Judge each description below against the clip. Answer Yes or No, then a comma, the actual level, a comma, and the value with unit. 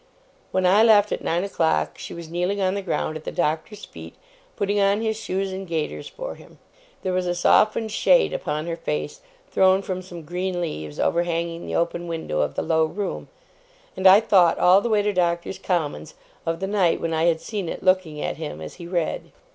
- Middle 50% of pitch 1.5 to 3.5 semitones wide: Yes, average, 3.1 semitones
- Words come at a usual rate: No, fast, 210 wpm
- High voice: No, medium, 180 Hz